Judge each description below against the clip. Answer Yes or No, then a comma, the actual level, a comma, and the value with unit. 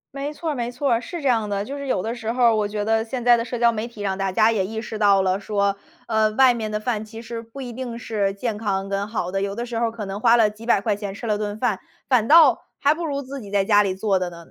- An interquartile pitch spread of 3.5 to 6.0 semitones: No, average, 3.0 semitones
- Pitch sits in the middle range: No, high, 220 Hz